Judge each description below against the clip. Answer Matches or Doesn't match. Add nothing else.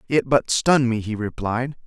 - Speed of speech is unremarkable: Matches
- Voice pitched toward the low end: Matches